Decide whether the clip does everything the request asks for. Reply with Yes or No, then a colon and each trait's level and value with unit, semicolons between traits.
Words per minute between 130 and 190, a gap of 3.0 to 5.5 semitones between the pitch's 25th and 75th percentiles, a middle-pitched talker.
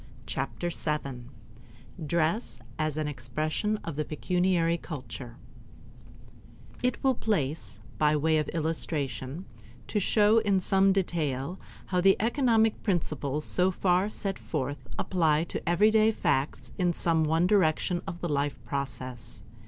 Yes: slow, 135 wpm; average, 5.0 semitones; medium, 165 Hz